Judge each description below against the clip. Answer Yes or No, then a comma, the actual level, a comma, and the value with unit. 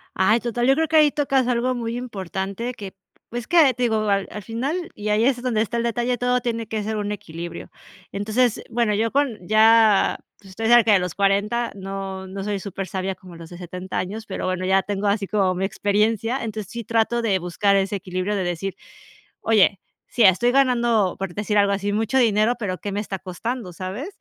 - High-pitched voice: Yes, high, 210 Hz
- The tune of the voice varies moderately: Yes, average, 3.6 semitones